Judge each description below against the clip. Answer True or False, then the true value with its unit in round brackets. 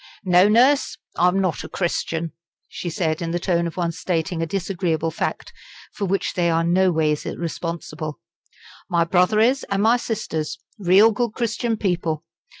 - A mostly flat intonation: False (3.3 semitones)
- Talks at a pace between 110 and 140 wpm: False (155 wpm)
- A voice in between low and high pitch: True (175 Hz)